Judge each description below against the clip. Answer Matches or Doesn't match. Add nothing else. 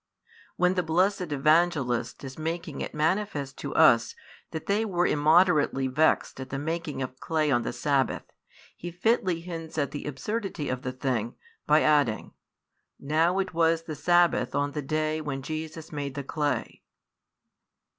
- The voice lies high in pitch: Doesn't match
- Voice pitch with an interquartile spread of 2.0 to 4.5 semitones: Matches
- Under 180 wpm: Matches